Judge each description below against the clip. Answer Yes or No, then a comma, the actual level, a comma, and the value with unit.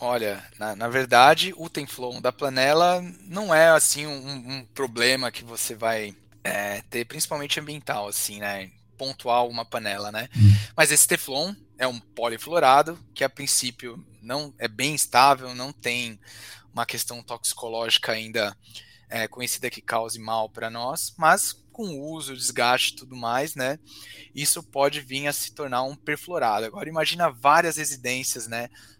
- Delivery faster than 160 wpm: No, average, 155 wpm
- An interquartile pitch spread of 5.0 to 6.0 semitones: No, average, 4.3 semitones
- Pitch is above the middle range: No, low, 125 Hz